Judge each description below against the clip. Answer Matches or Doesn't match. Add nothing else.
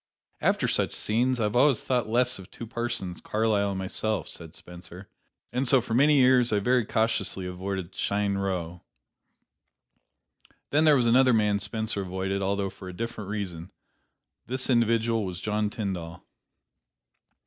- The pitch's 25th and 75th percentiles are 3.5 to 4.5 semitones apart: Matches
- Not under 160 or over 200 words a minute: Doesn't match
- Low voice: Matches